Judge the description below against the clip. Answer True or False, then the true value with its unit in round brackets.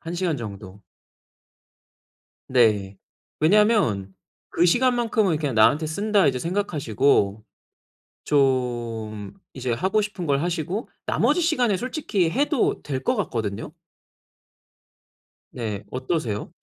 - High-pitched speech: False (150 Hz)